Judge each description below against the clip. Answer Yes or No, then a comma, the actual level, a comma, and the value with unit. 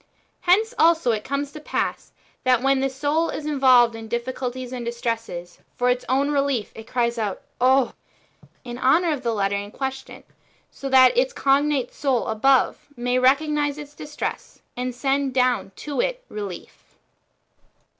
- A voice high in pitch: Yes, very high, 260 Hz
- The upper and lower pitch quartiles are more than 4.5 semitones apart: No, average, 3.1 semitones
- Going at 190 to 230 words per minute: No, average, 170 wpm